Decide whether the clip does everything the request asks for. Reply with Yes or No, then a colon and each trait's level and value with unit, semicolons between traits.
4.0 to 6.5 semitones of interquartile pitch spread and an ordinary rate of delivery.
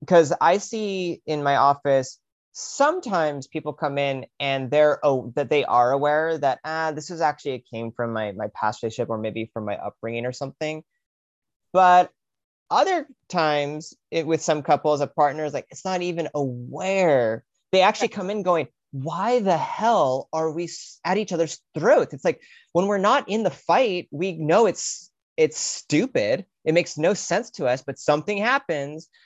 Yes: average, 4.9 semitones; average, 175 wpm